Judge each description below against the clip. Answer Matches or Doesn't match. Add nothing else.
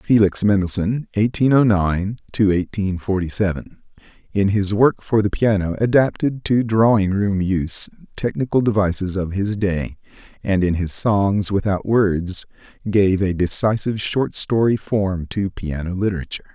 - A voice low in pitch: Matches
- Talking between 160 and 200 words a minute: Doesn't match